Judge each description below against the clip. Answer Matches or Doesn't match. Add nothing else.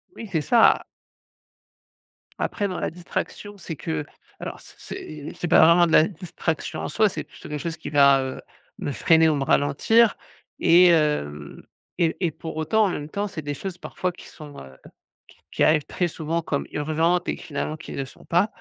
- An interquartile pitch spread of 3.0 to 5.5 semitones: Matches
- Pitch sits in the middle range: Matches